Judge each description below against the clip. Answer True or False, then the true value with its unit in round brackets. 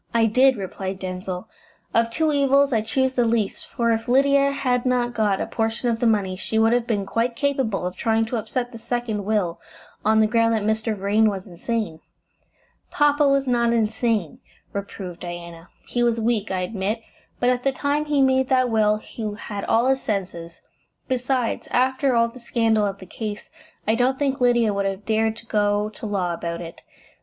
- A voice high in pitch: True (225 Hz)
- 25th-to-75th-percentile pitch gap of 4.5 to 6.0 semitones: False (3.4 semitones)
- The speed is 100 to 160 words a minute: False (195 wpm)